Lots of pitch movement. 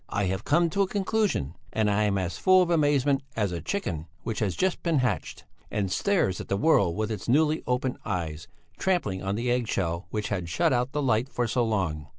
Yes: wide, 7.5 semitones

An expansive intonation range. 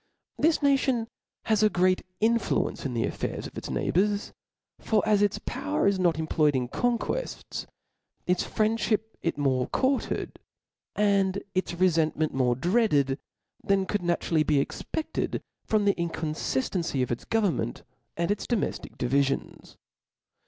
Yes: wide, 6.1 semitones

